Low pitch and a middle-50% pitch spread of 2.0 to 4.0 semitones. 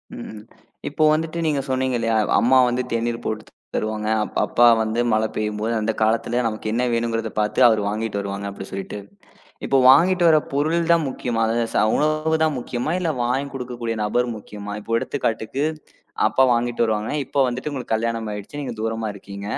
Yes: low, 115 Hz; average, 3.7 semitones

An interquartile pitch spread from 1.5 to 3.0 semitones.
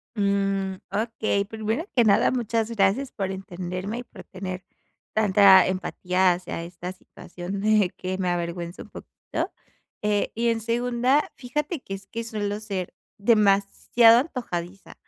No: average, 3.5 semitones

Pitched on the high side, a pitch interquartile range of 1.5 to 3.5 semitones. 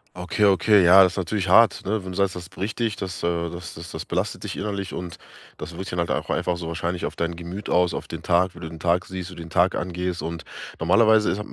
No: very low, 90 Hz; narrow, 2.2 semitones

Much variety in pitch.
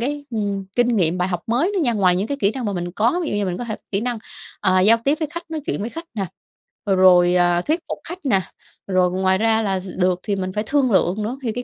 No: average, 4.7 semitones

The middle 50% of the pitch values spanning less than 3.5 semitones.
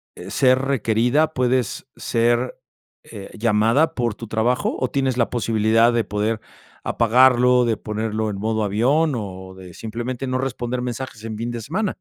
Yes: average, 2.7 semitones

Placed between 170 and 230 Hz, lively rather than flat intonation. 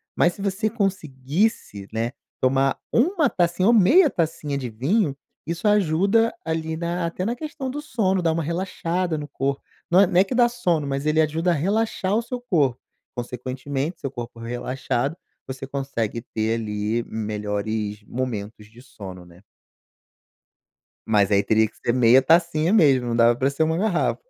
No: medium, 150 Hz; wide, 7.6 semitones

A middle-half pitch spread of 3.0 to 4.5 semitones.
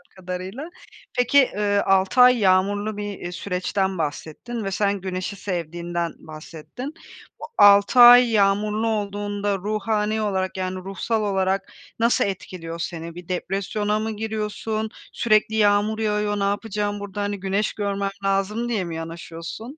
No: narrow, 2.4 semitones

